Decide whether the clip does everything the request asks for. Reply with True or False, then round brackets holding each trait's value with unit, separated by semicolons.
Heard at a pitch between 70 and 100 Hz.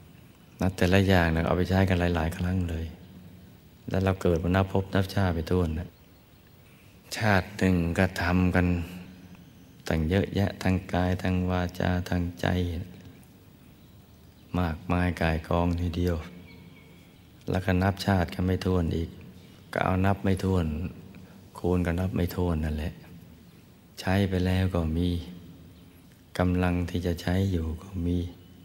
True (90 Hz)